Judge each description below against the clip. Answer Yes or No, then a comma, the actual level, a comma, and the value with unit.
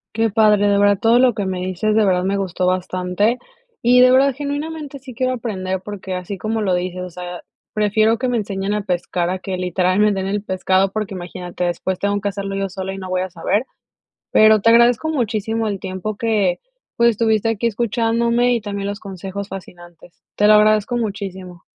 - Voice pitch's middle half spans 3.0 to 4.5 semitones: Yes, average, 3.3 semitones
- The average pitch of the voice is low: No, high, 205 Hz